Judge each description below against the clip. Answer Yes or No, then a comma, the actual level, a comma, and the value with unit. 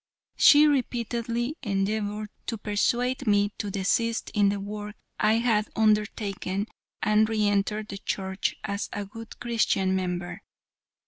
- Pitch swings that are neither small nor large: No, narrow, 2.3 semitones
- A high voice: Yes, high, 210 Hz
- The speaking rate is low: Yes, slow, 130 wpm